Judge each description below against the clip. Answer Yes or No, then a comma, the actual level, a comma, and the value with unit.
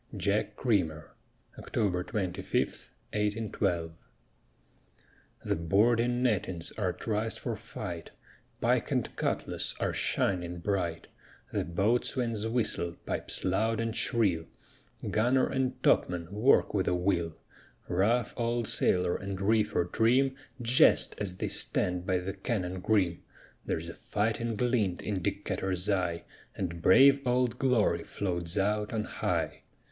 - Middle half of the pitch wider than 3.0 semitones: Yes, average, 4.2 semitones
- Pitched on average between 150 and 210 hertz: No, low, 100 Hz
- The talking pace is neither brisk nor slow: No, slow, 120 wpm